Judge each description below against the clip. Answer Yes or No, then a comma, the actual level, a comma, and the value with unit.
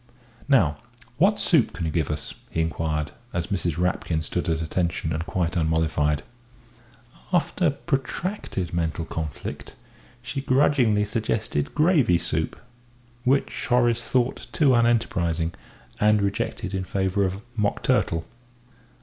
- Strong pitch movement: Yes, wide, 7.2 semitones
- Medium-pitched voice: No, very low, 95 Hz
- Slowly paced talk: Yes, slow, 125 wpm